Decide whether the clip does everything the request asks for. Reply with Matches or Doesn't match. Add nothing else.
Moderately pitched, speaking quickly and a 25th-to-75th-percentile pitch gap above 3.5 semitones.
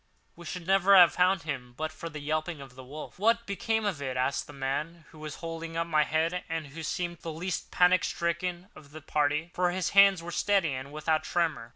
Doesn't match